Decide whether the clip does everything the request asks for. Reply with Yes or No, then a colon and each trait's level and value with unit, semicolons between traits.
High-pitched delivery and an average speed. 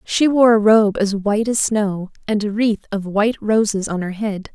No: high, 210 Hz; fast, 225 wpm